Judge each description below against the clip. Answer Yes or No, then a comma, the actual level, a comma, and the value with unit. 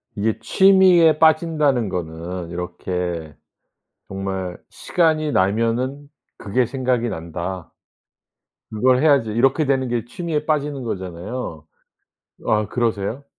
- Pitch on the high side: No, low, 115 Hz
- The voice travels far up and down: Yes, wide, 7.5 semitones